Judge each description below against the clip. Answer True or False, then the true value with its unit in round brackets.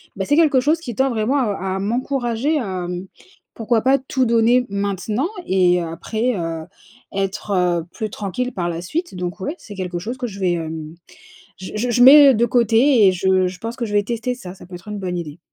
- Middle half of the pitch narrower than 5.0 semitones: False (5.3 semitones)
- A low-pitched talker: False (210 Hz)